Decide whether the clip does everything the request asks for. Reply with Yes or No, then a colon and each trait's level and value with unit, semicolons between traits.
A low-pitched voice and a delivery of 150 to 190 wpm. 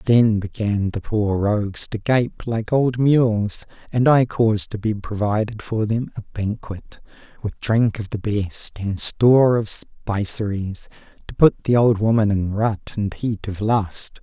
Yes: low, 110 Hz; average, 170 wpm